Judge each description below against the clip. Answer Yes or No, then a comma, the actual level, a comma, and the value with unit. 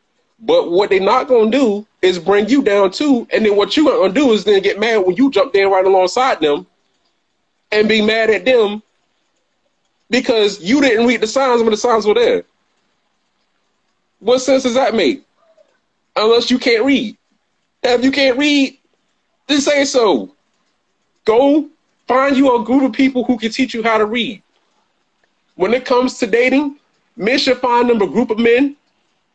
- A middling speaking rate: Yes, average, 180 wpm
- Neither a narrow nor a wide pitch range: Yes, average, 3.9 semitones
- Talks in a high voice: Yes, high, 245 Hz